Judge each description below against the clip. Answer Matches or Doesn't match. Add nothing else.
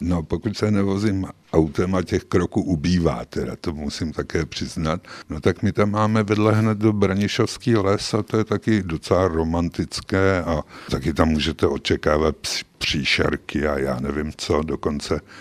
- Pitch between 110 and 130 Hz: Doesn't match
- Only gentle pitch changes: Doesn't match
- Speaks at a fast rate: Doesn't match